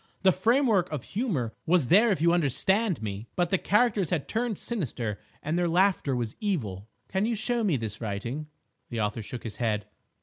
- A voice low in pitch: No, medium, 170 Hz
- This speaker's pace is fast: No, average, 190 wpm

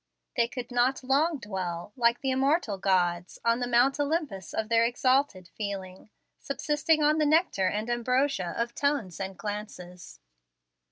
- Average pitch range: No, wide, 6.1 semitones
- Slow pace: No, average, 150 wpm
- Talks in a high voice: Yes, high, 235 Hz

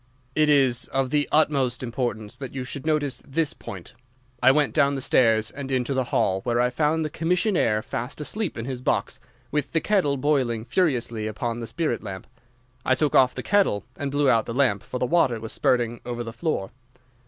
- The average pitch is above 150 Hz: No, low, 130 Hz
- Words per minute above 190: Yes, average, 200 wpm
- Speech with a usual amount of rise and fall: Yes, average, 3.9 semitones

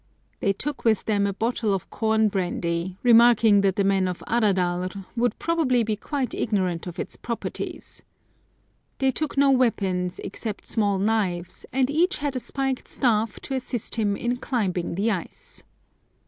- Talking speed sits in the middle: Yes, average, 160 wpm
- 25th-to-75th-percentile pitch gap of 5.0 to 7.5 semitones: No, average, 4.4 semitones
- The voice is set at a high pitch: Yes, high, 215 Hz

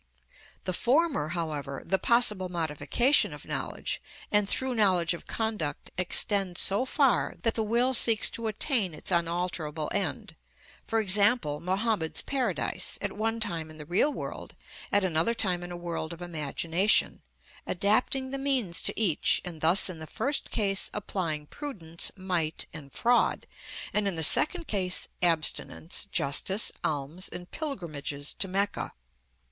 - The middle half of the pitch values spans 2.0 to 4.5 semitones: No, average, 5.3 semitones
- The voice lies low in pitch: No, medium, 185 Hz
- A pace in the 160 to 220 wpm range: No, average, 145 wpm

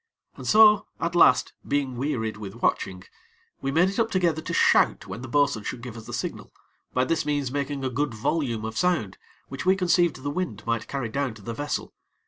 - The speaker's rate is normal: No, fast, 210 wpm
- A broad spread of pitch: Yes, wide, 6.2 semitones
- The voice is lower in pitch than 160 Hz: Yes, medium, 140 Hz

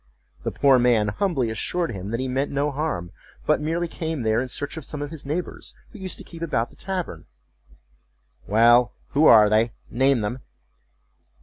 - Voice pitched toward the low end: Yes, low, 130 Hz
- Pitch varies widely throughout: Yes, wide, 6.1 semitones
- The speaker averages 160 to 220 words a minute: Yes, average, 170 wpm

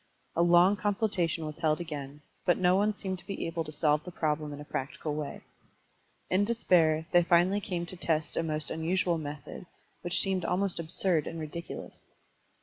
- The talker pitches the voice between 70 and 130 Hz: No, medium, 170 Hz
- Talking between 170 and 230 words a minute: Yes, average, 180 wpm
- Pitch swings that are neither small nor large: Yes, average, 3.1 semitones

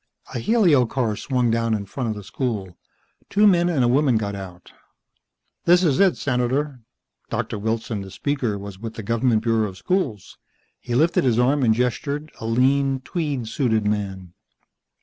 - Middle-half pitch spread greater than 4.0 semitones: Yes, average, 4.6 semitones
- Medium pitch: No, low, 120 Hz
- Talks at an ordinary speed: Yes, average, 170 wpm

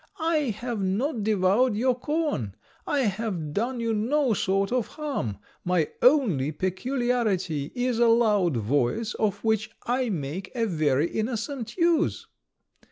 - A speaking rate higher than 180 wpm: No, slow, 135 wpm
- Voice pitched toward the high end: Yes, high, 220 Hz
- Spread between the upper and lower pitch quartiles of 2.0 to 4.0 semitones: No, average, 5.2 semitones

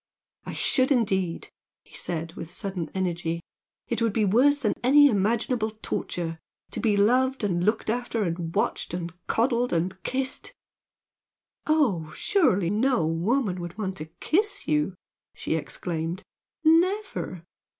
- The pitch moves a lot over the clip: Yes, wide, 6.6 semitones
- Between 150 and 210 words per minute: No, average, 140 wpm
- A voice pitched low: No, high, 205 Hz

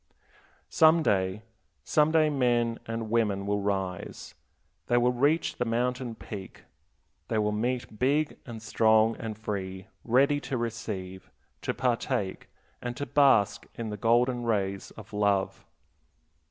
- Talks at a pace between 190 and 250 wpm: No, slow, 135 wpm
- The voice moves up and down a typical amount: Yes, average, 3.4 semitones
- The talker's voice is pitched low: Yes, low, 115 Hz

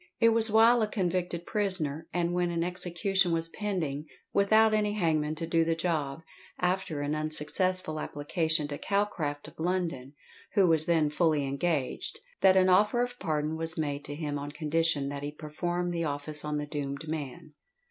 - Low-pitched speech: No, medium, 165 Hz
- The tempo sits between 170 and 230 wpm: Yes, average, 175 wpm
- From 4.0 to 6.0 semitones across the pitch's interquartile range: No, average, 3.6 semitones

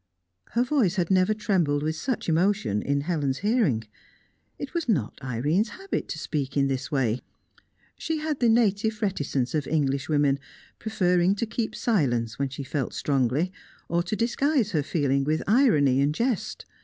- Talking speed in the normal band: Yes, average, 165 wpm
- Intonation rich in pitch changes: Yes, wide, 7.7 semitones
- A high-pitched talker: No, medium, 165 Hz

